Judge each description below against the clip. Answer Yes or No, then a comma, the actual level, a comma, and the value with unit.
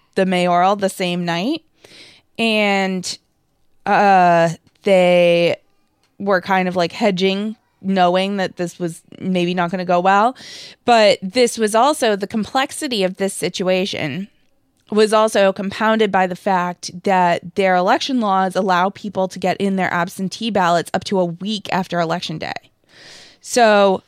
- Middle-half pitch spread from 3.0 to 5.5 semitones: No, narrow, 2.6 semitones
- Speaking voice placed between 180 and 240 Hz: Yes, high, 190 Hz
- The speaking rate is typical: Yes, average, 145 wpm